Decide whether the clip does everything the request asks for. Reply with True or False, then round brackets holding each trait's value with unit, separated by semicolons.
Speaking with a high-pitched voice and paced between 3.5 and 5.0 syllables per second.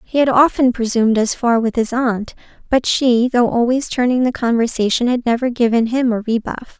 False (240 Hz; 5.2 syllables/s)